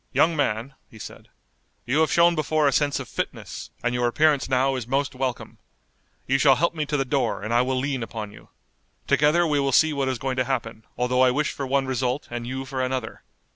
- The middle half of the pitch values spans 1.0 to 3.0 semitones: Yes, narrow, 2.6 semitones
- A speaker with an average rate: No, fast, 225 wpm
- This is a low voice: Yes, low, 130 Hz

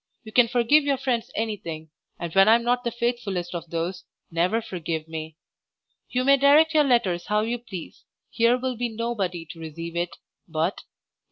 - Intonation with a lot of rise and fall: Yes, wide, 6.1 semitones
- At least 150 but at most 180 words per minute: No, average, 195 wpm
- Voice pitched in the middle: No, high, 215 Hz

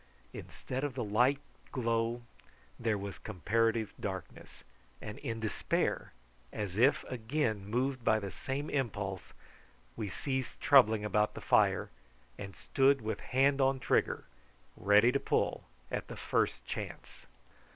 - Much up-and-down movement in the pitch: No, average, 4.0 semitones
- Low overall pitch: Yes, low, 115 Hz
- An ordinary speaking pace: No, slow, 130 wpm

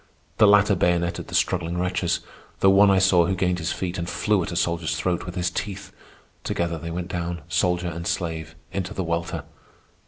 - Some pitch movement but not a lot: No, narrow, 1.7 semitones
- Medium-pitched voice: No, very low, 90 Hz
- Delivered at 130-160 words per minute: No, average, 195 wpm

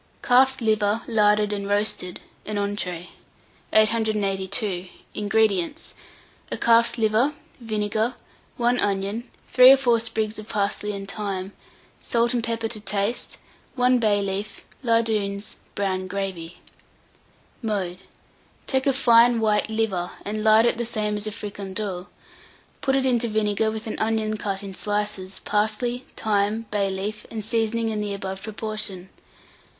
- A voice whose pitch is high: Yes, high, 215 Hz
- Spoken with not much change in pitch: Yes, narrow, 2.3 semitones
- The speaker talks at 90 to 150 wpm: Yes, slow, 135 wpm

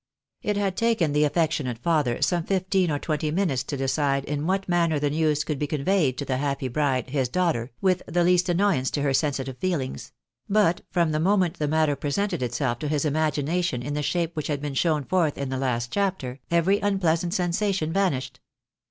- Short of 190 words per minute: No, average, 195 wpm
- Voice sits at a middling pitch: Yes, medium, 155 Hz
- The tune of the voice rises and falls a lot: No, average, 4.4 semitones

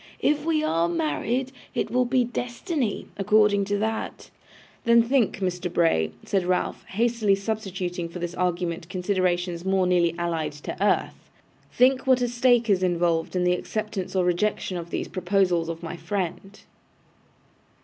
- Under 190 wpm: Yes, average, 150 wpm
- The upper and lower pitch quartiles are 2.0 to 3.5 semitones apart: No, average, 4.4 semitones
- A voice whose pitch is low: No, high, 190 Hz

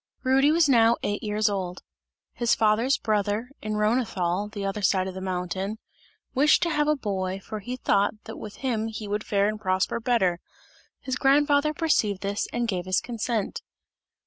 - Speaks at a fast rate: No, average, 175 wpm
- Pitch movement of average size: Yes, average, 4.1 semitones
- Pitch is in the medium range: No, high, 215 Hz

